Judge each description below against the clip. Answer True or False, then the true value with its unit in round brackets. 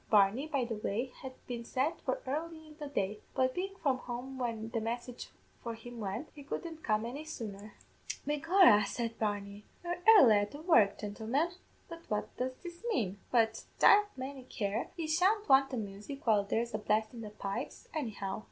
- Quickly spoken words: False (190 wpm)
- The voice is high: True (245 Hz)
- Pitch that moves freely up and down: True (5.7 semitones)